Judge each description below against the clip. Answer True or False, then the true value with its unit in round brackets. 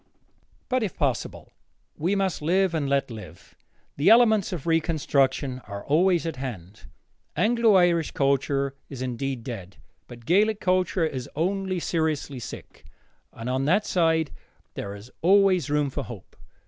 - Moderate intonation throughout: False (6.0 semitones)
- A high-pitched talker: False (155 Hz)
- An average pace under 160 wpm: True (145 wpm)